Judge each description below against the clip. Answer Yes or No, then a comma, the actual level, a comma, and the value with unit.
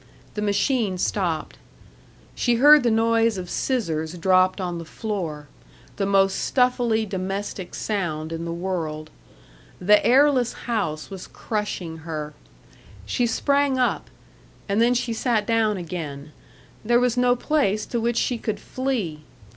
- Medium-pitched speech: No, high, 210 Hz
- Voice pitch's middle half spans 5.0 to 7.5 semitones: Yes, wide, 5.5 semitones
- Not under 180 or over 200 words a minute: No, average, 140 wpm